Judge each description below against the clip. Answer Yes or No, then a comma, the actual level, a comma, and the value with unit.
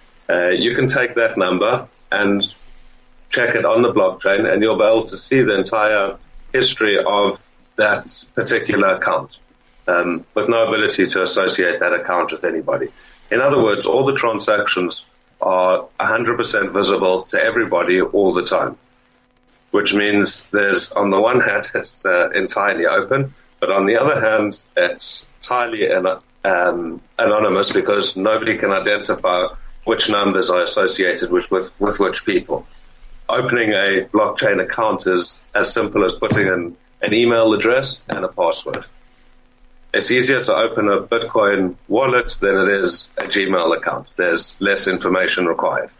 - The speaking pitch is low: Yes, low, 110 Hz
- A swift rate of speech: No, average, 150 wpm